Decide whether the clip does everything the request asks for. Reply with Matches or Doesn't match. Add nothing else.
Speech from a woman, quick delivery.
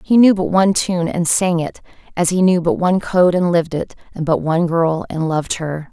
Matches